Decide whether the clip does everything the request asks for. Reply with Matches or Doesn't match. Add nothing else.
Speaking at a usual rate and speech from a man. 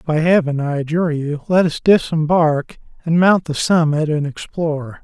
Matches